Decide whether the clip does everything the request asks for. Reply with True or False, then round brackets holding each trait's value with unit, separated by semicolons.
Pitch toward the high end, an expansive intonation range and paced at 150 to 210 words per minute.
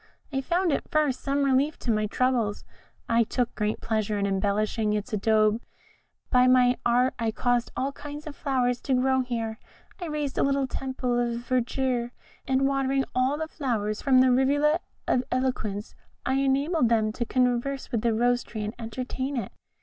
False (250 Hz; 3.1 semitones; 175 wpm)